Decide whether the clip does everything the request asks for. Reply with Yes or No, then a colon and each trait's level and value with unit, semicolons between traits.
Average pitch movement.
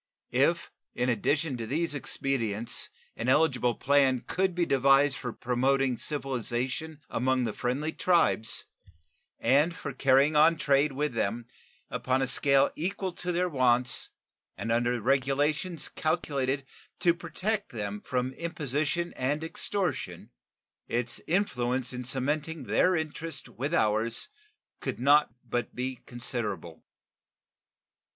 Yes: average, 4.1 semitones